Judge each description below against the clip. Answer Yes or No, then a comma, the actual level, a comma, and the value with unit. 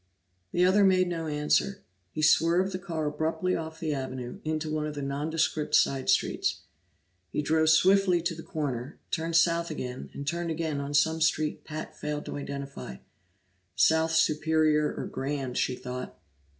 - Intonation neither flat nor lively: No, narrow, 2.3 semitones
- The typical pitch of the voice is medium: Yes, medium, 155 Hz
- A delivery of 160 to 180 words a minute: Yes, average, 165 wpm